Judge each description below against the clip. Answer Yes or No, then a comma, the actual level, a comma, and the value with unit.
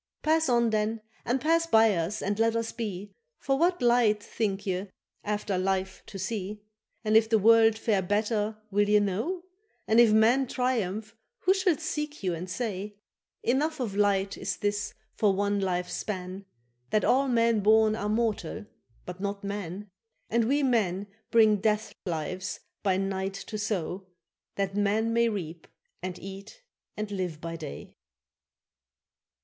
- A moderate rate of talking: Yes, average, 155 wpm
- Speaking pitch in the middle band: No, high, 210 Hz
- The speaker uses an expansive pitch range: No, average, 2.9 semitones